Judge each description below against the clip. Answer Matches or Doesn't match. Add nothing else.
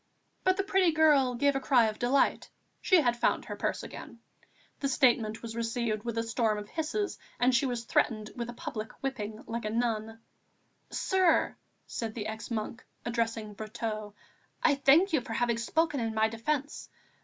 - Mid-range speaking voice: Doesn't match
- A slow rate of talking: Doesn't match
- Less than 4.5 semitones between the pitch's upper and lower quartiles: Matches